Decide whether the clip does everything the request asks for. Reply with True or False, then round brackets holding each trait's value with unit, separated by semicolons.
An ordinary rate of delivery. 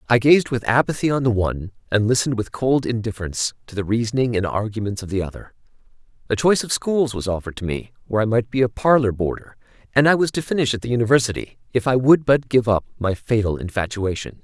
False (215 wpm)